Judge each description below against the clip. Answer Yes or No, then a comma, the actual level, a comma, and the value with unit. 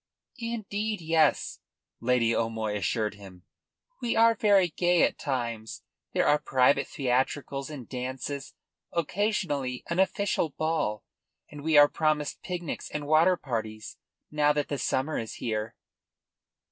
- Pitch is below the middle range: No, medium, 145 Hz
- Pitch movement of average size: No, wide, 5.9 semitones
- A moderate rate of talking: No, slow, 130 wpm